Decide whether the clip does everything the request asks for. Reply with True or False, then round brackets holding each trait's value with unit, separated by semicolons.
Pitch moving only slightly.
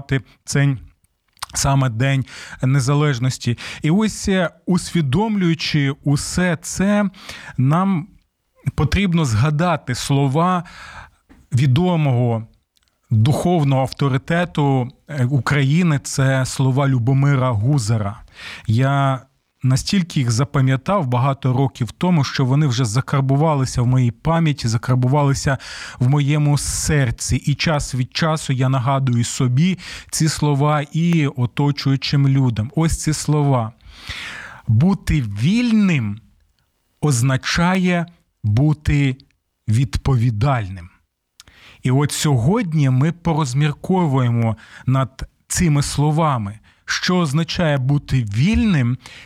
False (3.7 semitones)